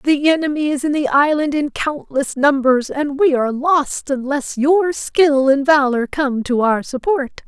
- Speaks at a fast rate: No, average, 175 wpm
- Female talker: Yes, female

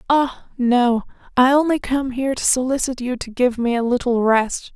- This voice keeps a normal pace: Yes, average, 190 wpm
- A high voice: Yes, very high, 250 Hz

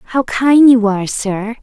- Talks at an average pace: Yes, average, 185 wpm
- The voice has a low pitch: No, high, 230 Hz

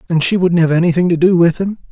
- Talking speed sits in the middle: No, fast, 280 wpm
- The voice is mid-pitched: Yes, medium, 170 Hz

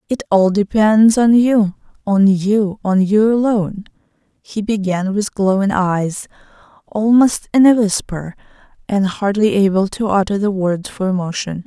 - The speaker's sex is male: No, female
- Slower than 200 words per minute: Yes, average, 145 wpm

